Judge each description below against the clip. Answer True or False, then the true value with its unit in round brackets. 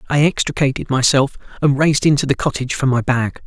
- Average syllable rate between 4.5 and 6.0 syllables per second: False (6.3 syllables/s)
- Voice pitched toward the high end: False (135 Hz)